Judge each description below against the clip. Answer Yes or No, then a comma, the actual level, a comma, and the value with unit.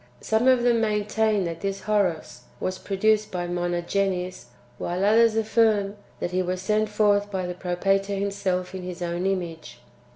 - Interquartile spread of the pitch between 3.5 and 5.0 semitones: No, average, 2.8 semitones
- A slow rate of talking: No, average, 170 wpm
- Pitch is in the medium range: No, high, 195 Hz